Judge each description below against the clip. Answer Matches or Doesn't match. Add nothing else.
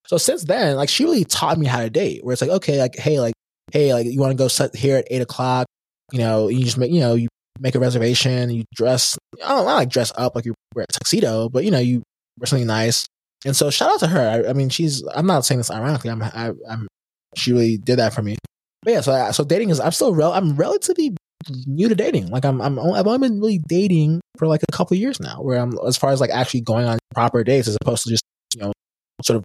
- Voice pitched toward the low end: Matches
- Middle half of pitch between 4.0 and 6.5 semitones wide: Matches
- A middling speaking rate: Doesn't match